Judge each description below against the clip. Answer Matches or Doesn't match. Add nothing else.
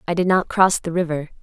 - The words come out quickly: Matches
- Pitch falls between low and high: Matches